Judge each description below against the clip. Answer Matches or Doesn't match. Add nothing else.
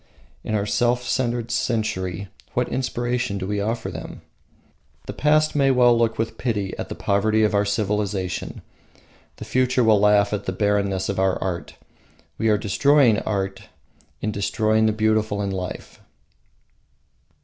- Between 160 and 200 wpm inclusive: Doesn't match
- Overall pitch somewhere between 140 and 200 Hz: Doesn't match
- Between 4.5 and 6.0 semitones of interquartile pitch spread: Doesn't match